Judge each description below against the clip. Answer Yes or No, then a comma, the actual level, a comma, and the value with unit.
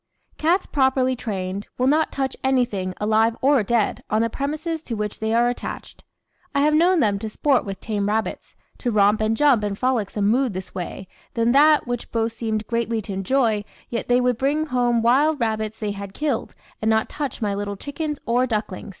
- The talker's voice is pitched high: Yes, high, 230 Hz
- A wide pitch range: No, average, 4.0 semitones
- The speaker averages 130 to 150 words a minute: No, average, 195 wpm